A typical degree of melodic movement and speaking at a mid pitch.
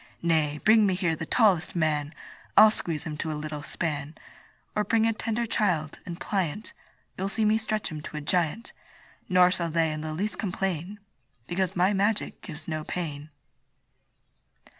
Yes: average, 5.0 semitones; medium, 175 Hz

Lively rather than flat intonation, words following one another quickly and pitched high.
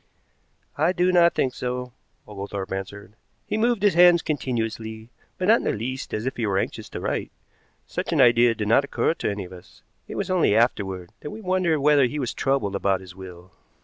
No: wide, 7.8 semitones; fast, 210 wpm; low, 120 Hz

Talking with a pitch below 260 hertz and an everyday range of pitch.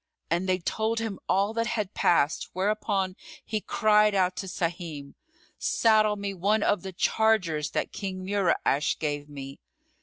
Yes: high, 190 Hz; average, 3.8 semitones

